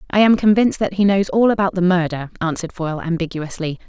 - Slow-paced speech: No, average, 200 wpm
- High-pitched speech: No, medium, 180 Hz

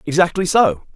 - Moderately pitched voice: Yes, medium, 160 Hz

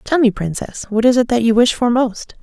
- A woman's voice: Yes, female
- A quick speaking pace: Yes, fast, 270 wpm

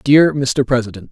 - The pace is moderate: Yes, average, 160 wpm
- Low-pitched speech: Yes, low, 130 Hz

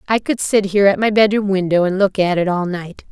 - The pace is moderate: No, fast, 270 wpm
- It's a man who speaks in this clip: No, female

